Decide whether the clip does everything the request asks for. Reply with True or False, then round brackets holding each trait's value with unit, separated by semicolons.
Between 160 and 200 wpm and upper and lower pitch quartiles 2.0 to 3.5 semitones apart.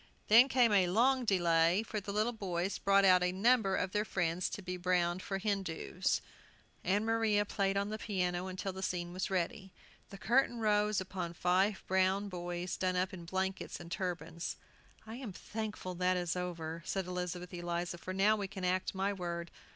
True (185 wpm; 2.6 semitones)